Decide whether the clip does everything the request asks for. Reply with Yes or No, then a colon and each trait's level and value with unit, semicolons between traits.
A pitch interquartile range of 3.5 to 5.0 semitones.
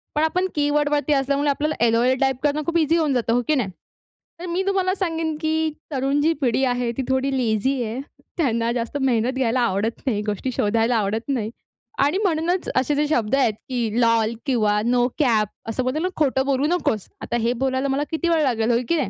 Yes: average, 4.4 semitones